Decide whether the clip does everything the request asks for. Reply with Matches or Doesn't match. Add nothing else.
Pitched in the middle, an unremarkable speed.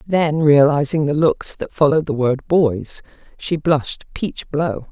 Matches